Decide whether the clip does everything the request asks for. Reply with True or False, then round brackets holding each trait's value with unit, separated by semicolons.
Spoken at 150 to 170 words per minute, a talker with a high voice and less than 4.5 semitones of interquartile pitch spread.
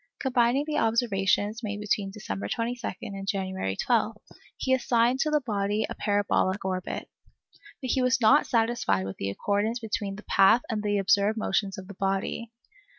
True (165 wpm; 210 Hz; 3.4 semitones)